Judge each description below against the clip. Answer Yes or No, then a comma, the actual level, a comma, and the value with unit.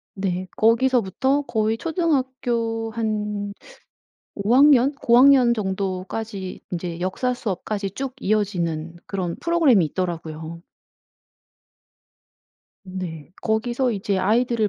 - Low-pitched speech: No, high, 215 Hz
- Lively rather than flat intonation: No, average, 4.8 semitones